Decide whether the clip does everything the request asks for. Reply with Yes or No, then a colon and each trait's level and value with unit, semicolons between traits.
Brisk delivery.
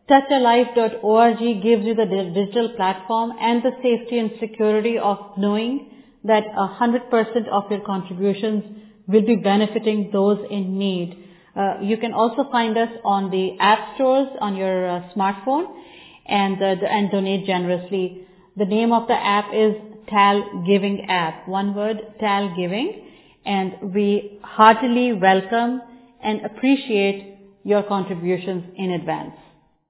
No: average, 135 wpm